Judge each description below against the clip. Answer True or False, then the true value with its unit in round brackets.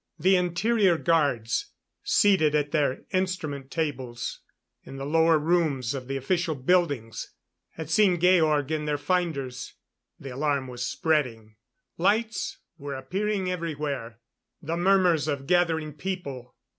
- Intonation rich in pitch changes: False (4.6 semitones)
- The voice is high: False (155 Hz)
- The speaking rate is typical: False (125 wpm)